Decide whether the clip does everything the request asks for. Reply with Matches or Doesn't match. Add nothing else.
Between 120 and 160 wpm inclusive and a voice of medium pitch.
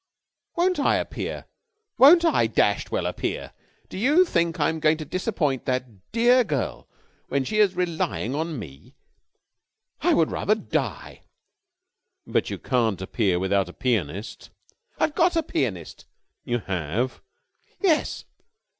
Matches